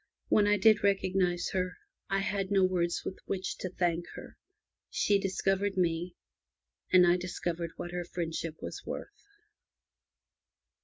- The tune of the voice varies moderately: No, narrow, 2.0 semitones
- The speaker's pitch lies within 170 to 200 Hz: Yes, medium, 185 Hz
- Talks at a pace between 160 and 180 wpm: No, average, 140 wpm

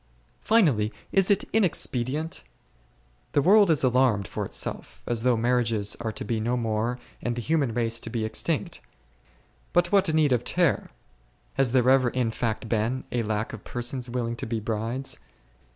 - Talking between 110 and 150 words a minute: No, average, 170 wpm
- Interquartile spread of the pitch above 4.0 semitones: No, average, 3.3 semitones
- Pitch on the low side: Yes, low, 120 Hz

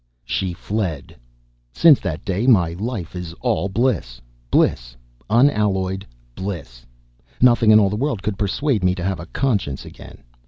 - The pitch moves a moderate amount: Yes, average, 4.7 semitones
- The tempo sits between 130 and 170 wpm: Yes, average, 150 wpm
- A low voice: Yes, very low, 95 Hz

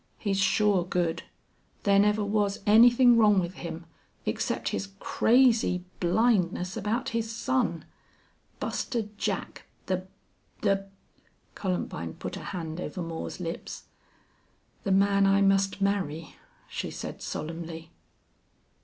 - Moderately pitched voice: No, high, 195 Hz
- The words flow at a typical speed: No, slow, 120 wpm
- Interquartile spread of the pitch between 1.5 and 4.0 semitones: Yes, average, 3.3 semitones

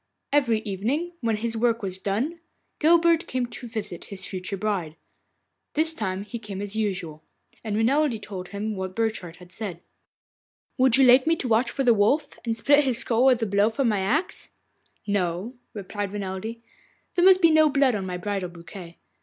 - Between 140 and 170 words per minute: No, average, 185 wpm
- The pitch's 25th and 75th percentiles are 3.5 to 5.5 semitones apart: Yes, average, 5.0 semitones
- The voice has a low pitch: No, high, 220 Hz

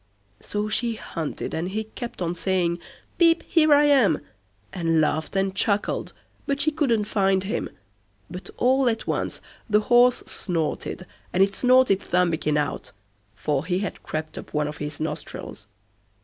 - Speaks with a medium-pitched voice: No, high, 195 Hz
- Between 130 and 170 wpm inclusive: Yes, average, 155 wpm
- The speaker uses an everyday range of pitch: No, wide, 6.5 semitones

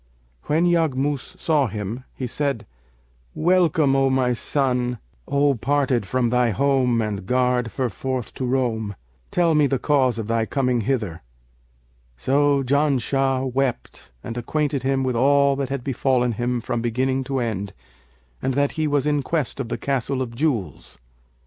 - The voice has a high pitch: No, low, 130 Hz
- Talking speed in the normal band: Yes, average, 155 wpm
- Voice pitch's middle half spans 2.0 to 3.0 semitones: Yes, average, 2.7 semitones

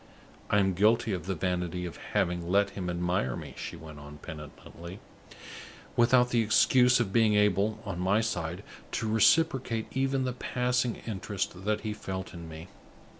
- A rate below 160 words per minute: No, average, 165 wpm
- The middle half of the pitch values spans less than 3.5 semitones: No, average, 4.6 semitones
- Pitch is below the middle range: Yes, low, 100 Hz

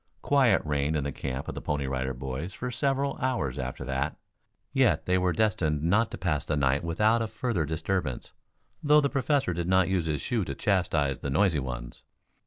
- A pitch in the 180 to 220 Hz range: No, very low, 85 Hz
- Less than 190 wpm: No, average, 195 wpm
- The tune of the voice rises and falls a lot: Yes, wide, 7.6 semitones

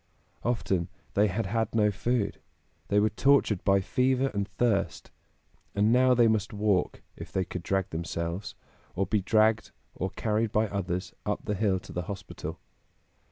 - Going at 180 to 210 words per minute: No, average, 160 wpm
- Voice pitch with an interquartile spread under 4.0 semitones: Yes, average, 2.8 semitones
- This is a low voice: Yes, low, 105 Hz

